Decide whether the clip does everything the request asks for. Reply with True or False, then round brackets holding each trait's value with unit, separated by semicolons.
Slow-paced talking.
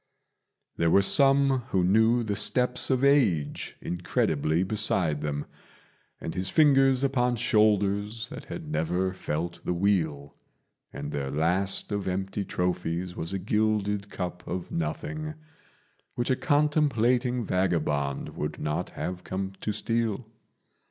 True (130 wpm)